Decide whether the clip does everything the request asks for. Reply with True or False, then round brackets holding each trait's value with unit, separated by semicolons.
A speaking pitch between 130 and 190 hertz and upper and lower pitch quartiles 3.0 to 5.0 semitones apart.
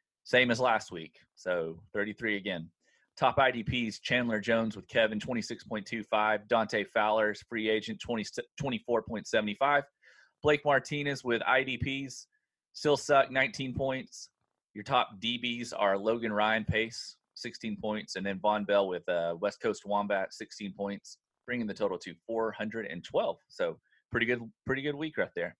False (115 Hz; 3.6 semitones)